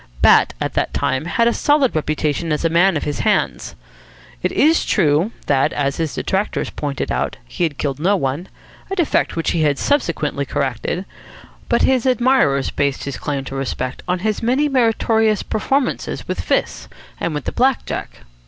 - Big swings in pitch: Yes, wide, 8.4 semitones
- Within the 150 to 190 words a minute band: Yes, average, 180 wpm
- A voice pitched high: No, medium, 170 Hz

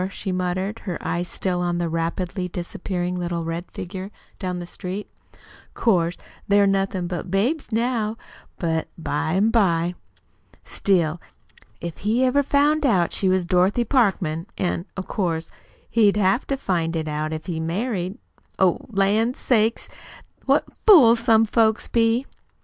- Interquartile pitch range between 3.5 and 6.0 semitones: Yes, average, 4.4 semitones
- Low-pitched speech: No, high, 190 Hz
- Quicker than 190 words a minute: No, average, 150 wpm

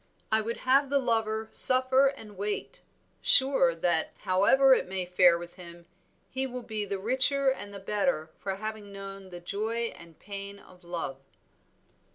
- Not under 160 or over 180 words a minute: Yes, average, 165 wpm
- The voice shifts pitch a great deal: Yes, wide, 5.7 semitones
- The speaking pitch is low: No, high, 205 Hz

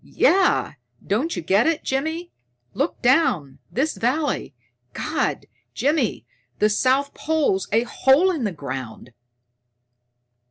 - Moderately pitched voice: No, very high, 265 Hz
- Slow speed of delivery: Yes, slow, 115 wpm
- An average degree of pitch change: No, wide, 8.0 semitones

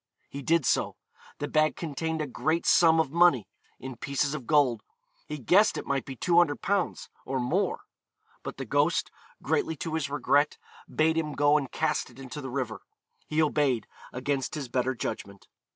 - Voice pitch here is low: No, medium, 145 Hz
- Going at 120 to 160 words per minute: No, average, 170 wpm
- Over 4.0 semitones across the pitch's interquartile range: No, average, 3.4 semitones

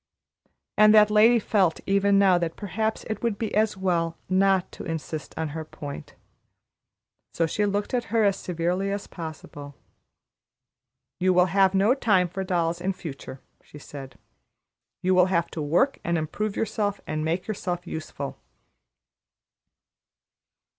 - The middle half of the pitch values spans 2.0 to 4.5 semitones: Yes, average, 3.7 semitones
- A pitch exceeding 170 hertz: Yes, medium, 185 Hz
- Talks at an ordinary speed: Yes, average, 145 wpm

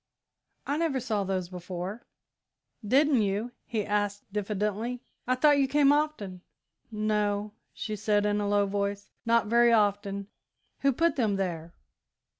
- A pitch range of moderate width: Yes, average, 3.3 semitones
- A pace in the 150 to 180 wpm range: No, average, 140 wpm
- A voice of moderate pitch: No, high, 210 Hz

